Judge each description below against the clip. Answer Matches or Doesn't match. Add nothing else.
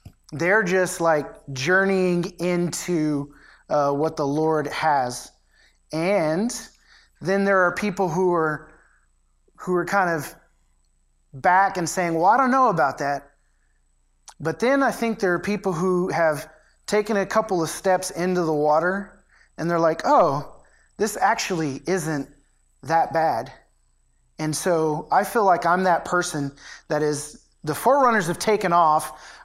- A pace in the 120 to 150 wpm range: Matches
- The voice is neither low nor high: Matches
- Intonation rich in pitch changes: Doesn't match